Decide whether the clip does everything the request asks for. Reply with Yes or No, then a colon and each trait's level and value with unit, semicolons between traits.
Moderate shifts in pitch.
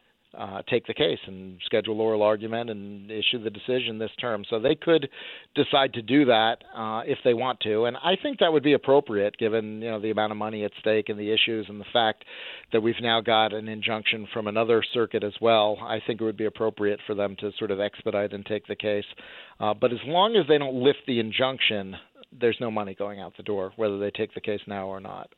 No: narrow, 2.3 semitones